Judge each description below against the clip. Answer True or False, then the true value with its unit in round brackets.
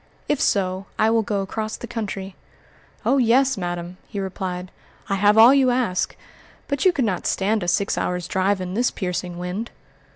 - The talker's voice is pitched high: True (200 Hz)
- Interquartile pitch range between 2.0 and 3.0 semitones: False (3.8 semitones)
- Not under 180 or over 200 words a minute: True (185 wpm)